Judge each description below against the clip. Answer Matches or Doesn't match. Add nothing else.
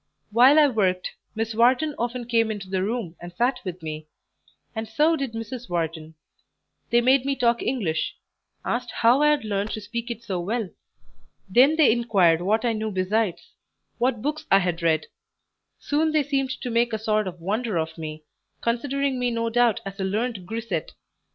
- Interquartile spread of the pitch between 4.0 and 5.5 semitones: Matches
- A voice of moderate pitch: Doesn't match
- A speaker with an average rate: Matches